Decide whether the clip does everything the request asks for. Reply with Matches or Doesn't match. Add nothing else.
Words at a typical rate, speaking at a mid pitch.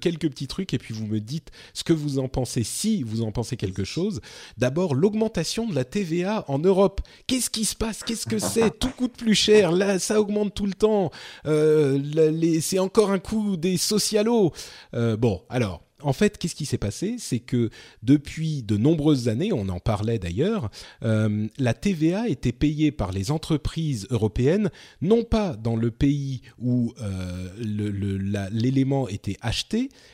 Matches